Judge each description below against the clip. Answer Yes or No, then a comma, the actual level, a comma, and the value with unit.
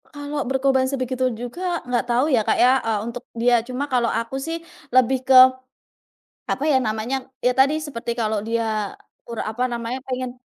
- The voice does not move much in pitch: Yes, narrow, 2.3 semitones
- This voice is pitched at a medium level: No, very high, 250 Hz